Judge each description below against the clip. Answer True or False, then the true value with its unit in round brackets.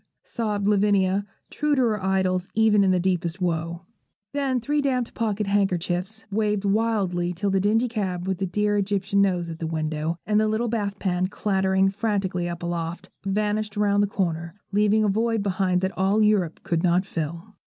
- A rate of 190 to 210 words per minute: False (180 wpm)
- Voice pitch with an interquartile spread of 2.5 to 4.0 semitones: True (2.9 semitones)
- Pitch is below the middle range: False (195 Hz)